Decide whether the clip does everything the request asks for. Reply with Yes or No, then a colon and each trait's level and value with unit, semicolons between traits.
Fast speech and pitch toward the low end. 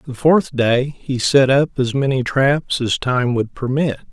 No: average, 190 wpm; low, 130 Hz